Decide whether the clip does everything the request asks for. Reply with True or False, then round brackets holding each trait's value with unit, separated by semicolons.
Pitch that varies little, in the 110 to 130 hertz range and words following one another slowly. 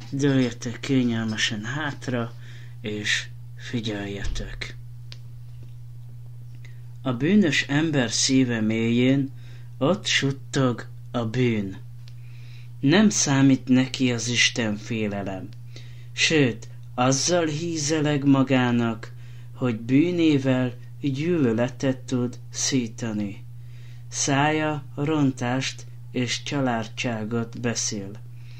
True (1.7 semitones; 120 Hz; 70 wpm)